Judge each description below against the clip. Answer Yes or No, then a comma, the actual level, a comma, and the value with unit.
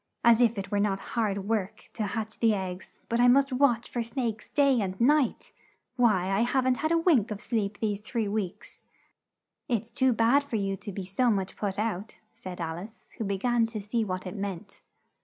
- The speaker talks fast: Yes, fast, 210 wpm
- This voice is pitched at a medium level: No, high, 220 Hz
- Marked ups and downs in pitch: No, average, 3.4 semitones